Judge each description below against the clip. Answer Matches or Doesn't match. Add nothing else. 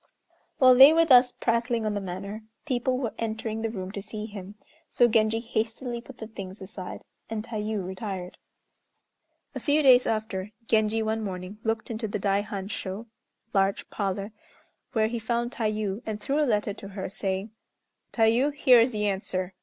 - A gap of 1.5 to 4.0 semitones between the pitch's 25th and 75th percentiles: Matches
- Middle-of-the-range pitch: Doesn't match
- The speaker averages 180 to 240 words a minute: Doesn't match